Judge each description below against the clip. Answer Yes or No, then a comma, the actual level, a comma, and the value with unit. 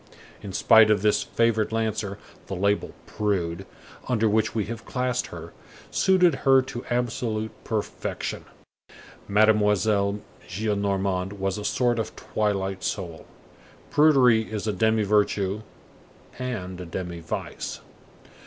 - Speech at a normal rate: No, slow, 120 wpm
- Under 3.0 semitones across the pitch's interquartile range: Yes, narrow, 2.5 semitones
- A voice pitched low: Yes, low, 105 Hz